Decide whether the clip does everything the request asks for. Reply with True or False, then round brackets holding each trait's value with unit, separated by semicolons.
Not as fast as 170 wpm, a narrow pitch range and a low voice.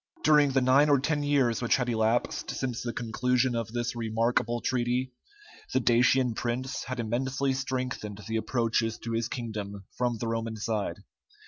True (160 wpm; 2.3 semitones; 120 Hz)